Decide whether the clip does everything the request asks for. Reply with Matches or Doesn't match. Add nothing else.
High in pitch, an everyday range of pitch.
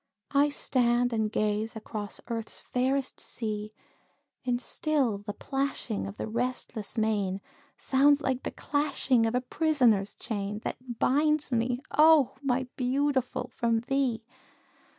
Matches